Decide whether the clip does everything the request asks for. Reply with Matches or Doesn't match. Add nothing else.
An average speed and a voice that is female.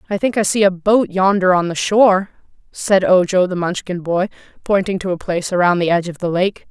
Doesn't match